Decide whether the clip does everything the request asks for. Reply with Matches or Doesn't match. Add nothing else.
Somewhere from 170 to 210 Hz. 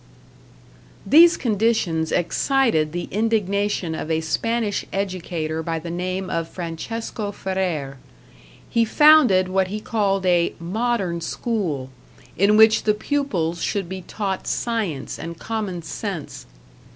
Matches